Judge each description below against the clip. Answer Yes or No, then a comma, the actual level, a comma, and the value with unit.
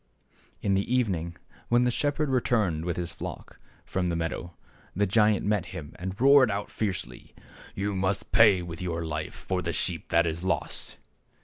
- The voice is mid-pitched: No, very low, 95 Hz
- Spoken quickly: No, average, 180 wpm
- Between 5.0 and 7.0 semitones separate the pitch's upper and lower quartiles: No, average, 4.2 semitones